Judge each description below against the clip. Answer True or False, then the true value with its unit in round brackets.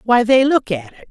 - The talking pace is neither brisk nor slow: False (270 wpm)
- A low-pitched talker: False (230 Hz)